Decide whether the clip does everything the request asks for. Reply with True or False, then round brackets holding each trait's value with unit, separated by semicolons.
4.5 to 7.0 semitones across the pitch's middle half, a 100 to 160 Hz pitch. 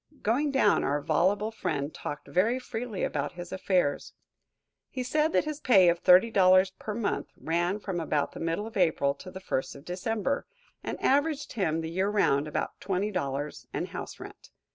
False (5.4 semitones; 185 Hz)